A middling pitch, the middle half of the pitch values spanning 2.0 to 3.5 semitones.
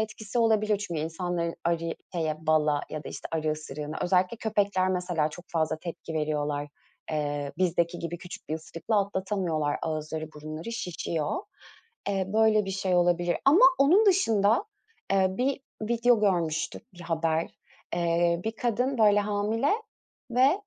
No: medium, 175 Hz; average, 5.0 semitones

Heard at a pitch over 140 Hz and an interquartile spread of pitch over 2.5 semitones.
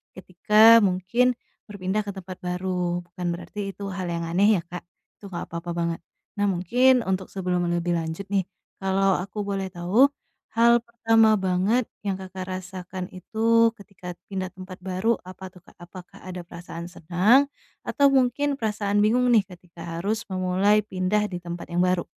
Yes: high, 190 Hz; average, 2.9 semitones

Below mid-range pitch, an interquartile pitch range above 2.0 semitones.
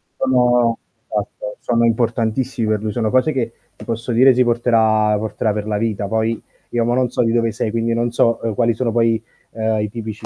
No: low, 115 Hz; narrow, 1.7 semitones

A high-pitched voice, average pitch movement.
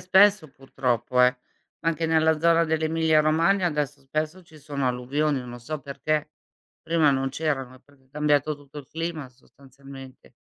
No: medium, 150 Hz; average, 3.1 semitones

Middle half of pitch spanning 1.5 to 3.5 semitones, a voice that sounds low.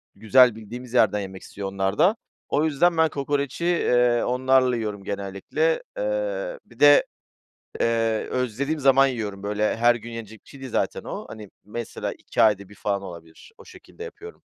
No: wide, 5.5 semitones; low, 120 Hz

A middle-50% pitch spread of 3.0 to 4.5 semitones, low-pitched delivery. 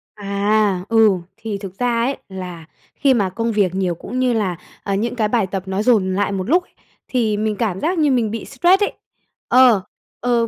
No: average, 3.9 semitones; high, 215 Hz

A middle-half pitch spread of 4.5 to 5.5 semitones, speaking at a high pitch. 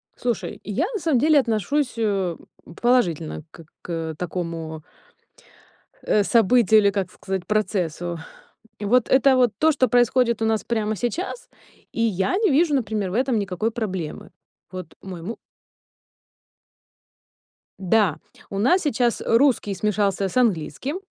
Yes: average, 5.2 semitones; high, 215 Hz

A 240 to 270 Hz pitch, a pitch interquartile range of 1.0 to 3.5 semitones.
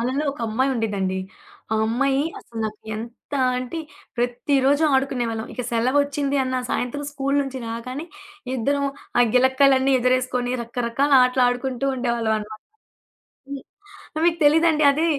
Yes: very high, 260 Hz; average, 2.9 semitones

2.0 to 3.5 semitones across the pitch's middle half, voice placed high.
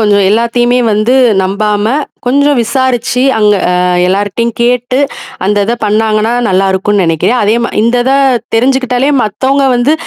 Yes: average, 3.2 semitones; high, 230 Hz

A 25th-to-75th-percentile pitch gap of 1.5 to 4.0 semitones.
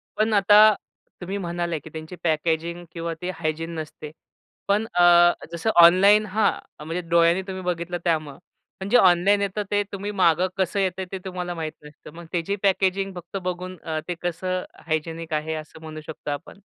Yes: average, 2.8 semitones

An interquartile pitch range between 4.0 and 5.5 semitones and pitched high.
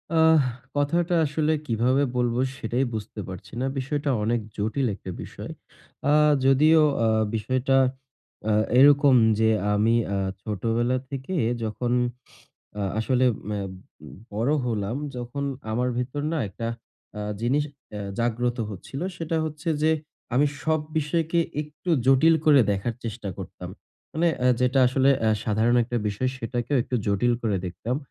No: average, 4.3 semitones; low, 125 Hz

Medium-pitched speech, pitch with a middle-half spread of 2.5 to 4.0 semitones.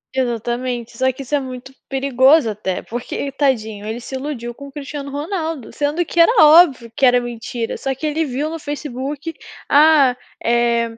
No: very high, 265 Hz; average, 3.5 semitones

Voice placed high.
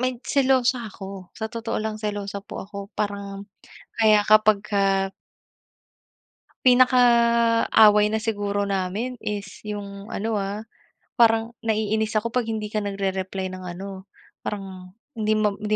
Yes: high, 210 Hz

